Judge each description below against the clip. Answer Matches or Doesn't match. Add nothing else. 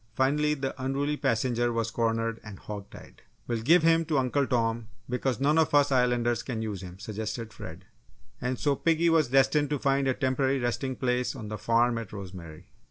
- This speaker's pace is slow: Doesn't match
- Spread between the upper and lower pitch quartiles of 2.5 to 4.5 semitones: Matches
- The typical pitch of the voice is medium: Doesn't match